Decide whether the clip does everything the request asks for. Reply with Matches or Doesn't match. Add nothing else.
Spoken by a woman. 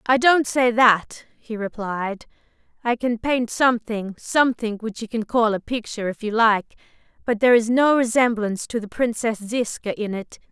Matches